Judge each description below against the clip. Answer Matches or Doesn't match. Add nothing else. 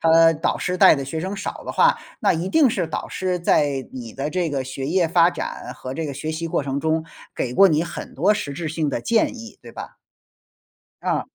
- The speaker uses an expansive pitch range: Doesn't match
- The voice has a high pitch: Doesn't match